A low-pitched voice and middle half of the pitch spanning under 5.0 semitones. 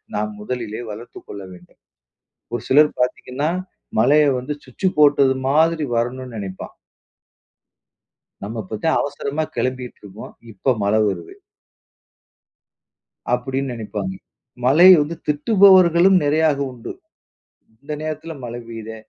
No: low, 130 Hz; average, 5.3 semitones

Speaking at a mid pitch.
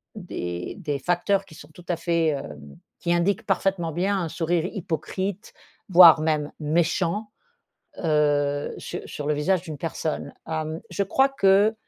Yes: medium, 170 Hz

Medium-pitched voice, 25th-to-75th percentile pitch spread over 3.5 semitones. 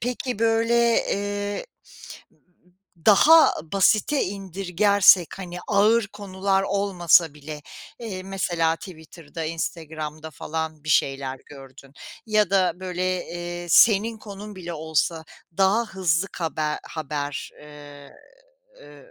Yes: medium, 180 Hz; average, 4.3 semitones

